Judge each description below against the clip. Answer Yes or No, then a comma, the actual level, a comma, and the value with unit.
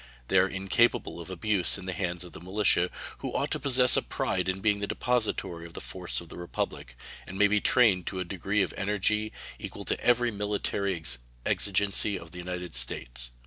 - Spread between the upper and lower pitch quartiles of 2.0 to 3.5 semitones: Yes, average, 2.9 semitones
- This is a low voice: Yes, very low, 95 Hz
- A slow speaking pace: No, average, 200 wpm